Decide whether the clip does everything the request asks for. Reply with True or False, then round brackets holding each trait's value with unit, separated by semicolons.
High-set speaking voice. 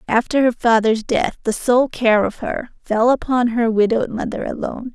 True (235 Hz)